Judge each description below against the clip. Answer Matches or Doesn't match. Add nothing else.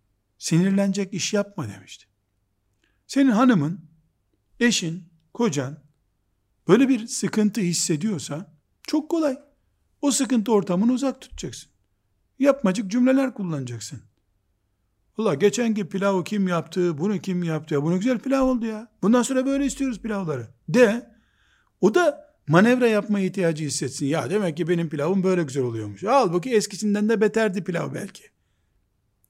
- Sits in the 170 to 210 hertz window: Matches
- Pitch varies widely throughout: Matches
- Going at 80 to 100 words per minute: Doesn't match